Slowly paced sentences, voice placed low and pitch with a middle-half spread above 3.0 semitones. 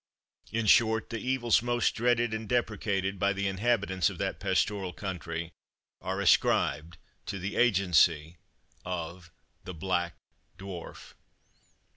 Yes: slow, 120 wpm; very low, 95 Hz; average, 3.8 semitones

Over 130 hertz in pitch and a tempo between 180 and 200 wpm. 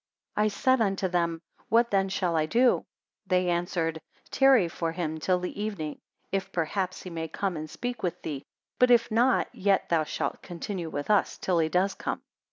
Yes: medium, 185 Hz; average, 185 wpm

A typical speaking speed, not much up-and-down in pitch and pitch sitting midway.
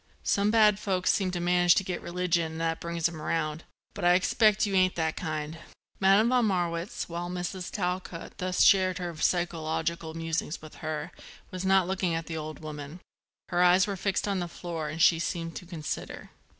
Yes: average, 190 wpm; narrow, 2.3 semitones; medium, 175 Hz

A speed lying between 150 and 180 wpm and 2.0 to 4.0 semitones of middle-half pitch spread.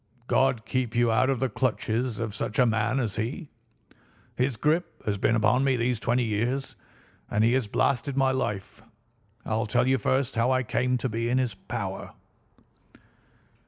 Yes: average, 175 wpm; average, 2.7 semitones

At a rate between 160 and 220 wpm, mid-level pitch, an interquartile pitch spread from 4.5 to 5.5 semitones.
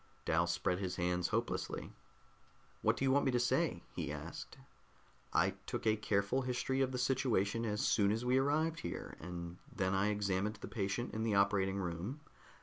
No: average, 180 wpm; low, 105 Hz; average, 4.8 semitones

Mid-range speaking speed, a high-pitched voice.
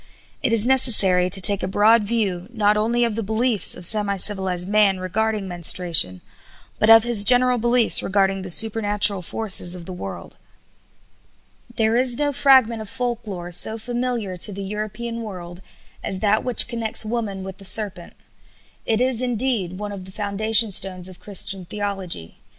Yes: average, 165 wpm; high, 210 Hz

